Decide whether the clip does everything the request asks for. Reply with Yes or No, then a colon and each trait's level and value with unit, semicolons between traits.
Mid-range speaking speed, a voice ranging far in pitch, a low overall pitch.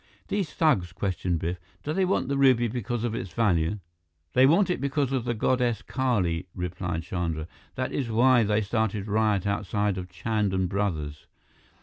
Yes: average, 170 wpm; wide, 5.7 semitones; low, 105 Hz